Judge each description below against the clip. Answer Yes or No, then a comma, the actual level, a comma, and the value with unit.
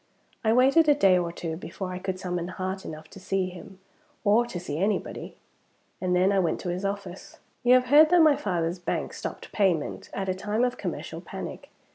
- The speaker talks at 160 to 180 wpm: No, fast, 205 wpm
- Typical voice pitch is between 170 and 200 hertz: Yes, high, 190 Hz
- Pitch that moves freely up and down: No, average, 3.8 semitones